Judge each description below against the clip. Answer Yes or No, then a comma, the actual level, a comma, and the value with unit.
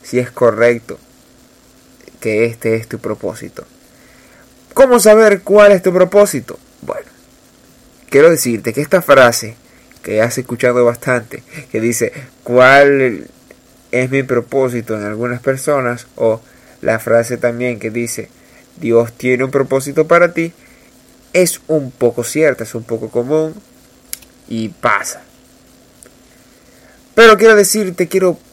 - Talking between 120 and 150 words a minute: Yes, slow, 125 wpm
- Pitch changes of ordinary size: Yes, average, 4.8 semitones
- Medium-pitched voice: No, low, 125 Hz